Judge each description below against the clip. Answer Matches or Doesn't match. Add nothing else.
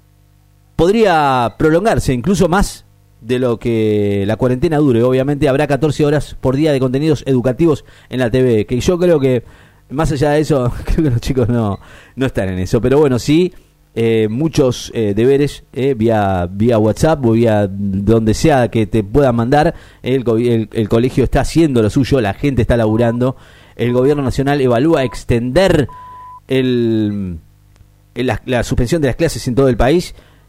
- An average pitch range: Matches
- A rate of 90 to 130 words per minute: Doesn't match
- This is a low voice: Matches